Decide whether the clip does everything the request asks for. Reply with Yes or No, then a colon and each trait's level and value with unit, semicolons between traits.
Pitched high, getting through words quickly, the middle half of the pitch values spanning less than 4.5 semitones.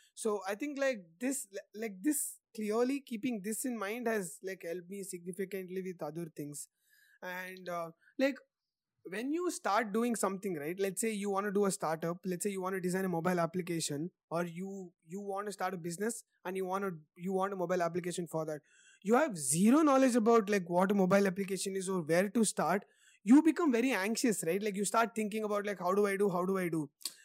Yes: high, 195 Hz; fast, 220 wpm; average, 3.9 semitones